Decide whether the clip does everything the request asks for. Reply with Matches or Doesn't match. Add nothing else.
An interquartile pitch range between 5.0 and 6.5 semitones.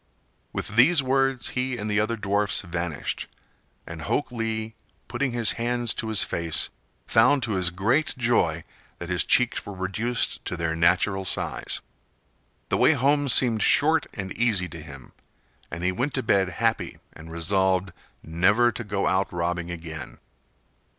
Matches